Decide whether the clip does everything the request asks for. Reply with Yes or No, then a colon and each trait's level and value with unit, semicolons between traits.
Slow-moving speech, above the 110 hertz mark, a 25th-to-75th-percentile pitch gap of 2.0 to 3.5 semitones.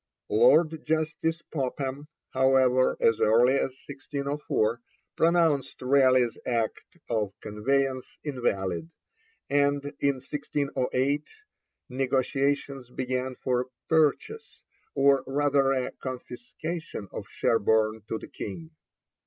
Yes: slow, 95 wpm; low, 135 Hz; narrow, 2.4 semitones